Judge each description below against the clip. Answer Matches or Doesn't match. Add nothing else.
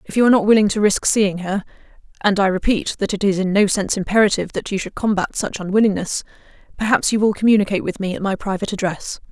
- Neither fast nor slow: Doesn't match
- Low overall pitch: Doesn't match